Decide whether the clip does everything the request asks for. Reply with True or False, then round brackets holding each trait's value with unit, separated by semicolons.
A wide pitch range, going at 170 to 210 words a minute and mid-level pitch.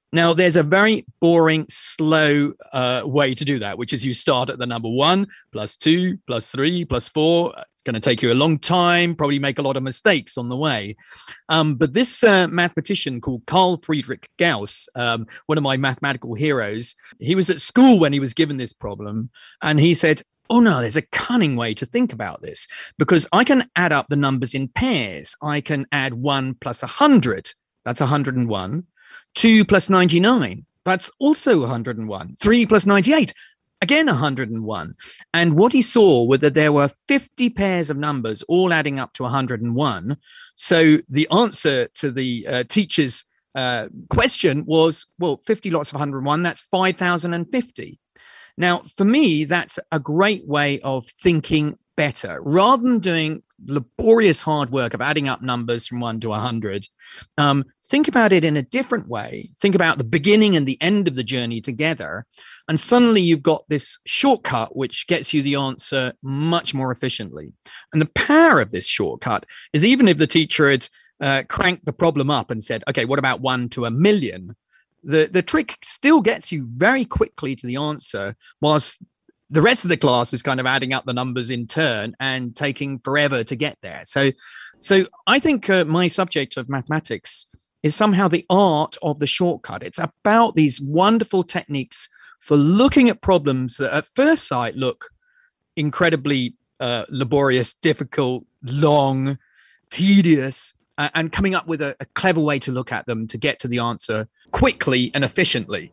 True (5.9 semitones; 180 wpm; 150 Hz)